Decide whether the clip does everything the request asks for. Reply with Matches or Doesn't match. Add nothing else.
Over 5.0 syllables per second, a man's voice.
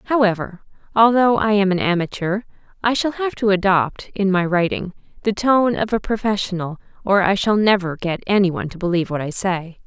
Doesn't match